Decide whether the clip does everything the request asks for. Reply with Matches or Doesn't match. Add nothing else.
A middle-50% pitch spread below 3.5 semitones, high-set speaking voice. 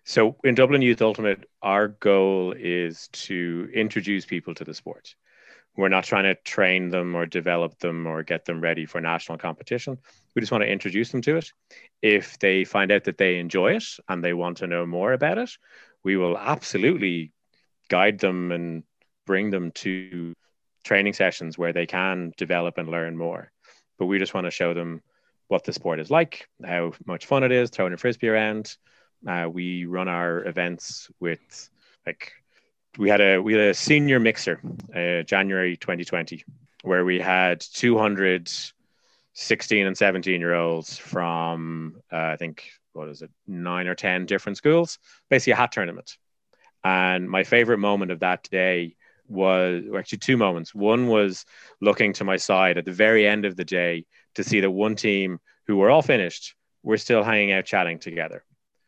Doesn't match